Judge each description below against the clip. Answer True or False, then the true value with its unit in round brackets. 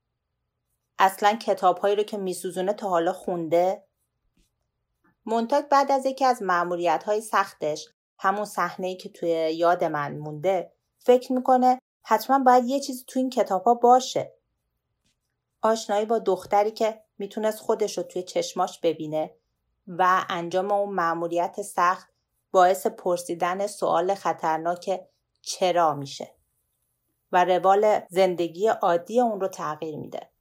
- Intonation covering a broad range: False (3.7 semitones)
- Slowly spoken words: False (120 wpm)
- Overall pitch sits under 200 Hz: True (190 Hz)